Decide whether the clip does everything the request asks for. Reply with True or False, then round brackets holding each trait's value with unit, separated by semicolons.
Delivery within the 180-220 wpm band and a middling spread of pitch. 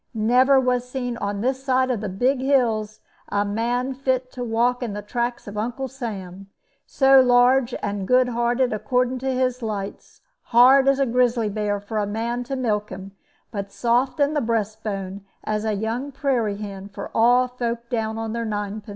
True (185 wpm; 3.3 semitones)